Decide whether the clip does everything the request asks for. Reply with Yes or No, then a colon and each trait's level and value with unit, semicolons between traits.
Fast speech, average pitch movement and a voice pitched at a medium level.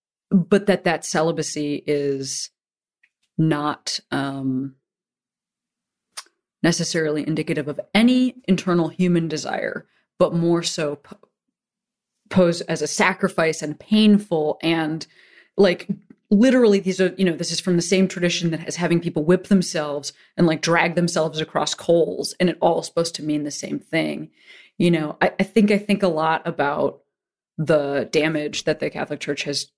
No: average, 155 wpm; average, 3.8 semitones; medium, 170 Hz